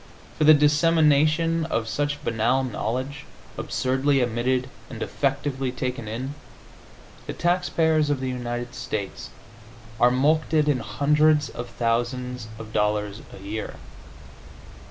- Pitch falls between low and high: No, low, 130 Hz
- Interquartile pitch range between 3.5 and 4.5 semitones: Yes, average, 3.9 semitones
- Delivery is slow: Yes, slow, 115 wpm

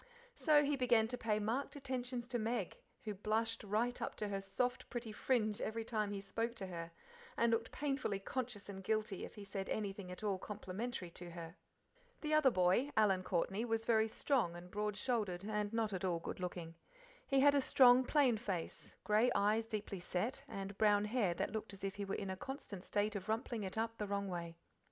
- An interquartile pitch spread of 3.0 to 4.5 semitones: Yes, average, 3.5 semitones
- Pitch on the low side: No, high, 215 Hz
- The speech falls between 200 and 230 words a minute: Yes, fast, 205 wpm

